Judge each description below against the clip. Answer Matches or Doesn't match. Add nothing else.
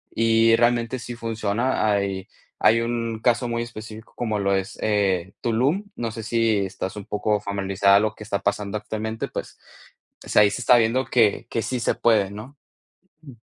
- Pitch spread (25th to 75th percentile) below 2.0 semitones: Doesn't match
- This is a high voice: Doesn't match